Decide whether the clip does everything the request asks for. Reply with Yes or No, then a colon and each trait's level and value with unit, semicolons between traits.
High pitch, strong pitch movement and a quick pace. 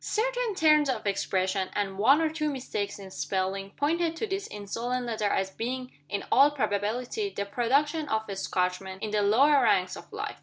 No: high, 230 Hz; wide, 6.8 semitones; average, 185 wpm